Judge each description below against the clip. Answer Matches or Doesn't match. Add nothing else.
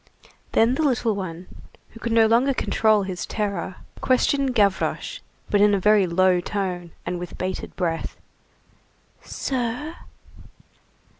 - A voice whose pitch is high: Matches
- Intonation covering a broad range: Doesn't match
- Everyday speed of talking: Doesn't match